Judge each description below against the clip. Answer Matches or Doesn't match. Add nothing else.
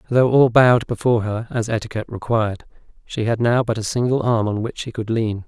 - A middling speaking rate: Doesn't match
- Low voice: Matches